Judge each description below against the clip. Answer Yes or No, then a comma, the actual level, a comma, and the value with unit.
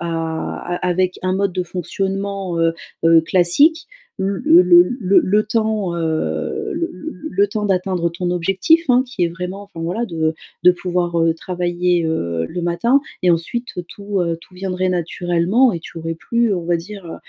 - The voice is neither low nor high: Yes, medium, 180 Hz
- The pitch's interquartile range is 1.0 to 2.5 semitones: No, average, 2.9 semitones